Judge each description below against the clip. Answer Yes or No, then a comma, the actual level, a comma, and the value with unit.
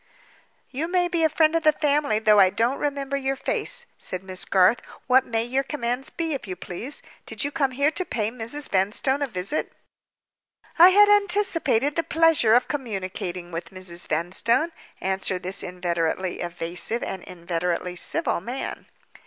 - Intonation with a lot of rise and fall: Yes, wide, 8.0 semitones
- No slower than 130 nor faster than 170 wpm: Yes, average, 165 wpm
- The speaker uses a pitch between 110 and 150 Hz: No, high, 235 Hz